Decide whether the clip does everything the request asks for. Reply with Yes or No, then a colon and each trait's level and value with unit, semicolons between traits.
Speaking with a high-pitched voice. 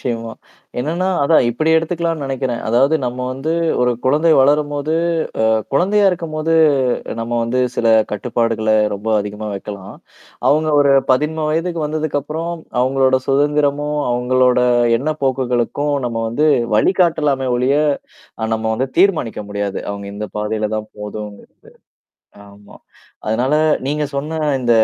No: low, 135 Hz